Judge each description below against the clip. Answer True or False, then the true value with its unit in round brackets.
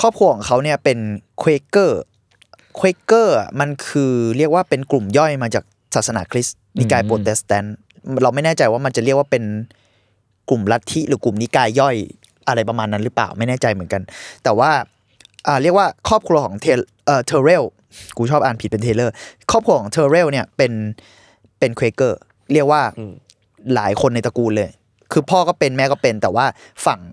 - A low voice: True (120 Hz)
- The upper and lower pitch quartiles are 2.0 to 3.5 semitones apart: False (5.0 semitones)